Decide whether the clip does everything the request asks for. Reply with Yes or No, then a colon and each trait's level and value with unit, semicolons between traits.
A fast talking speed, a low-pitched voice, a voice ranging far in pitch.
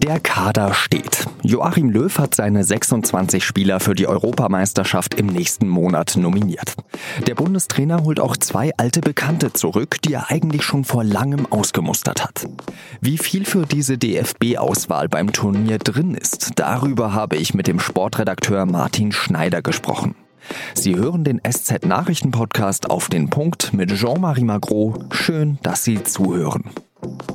No: average, 140 wpm; low, 120 Hz; wide, 6.5 semitones